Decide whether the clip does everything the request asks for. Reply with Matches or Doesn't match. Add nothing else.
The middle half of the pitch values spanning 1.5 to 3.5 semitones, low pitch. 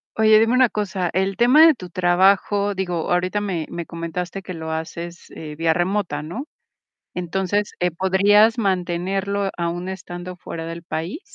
Doesn't match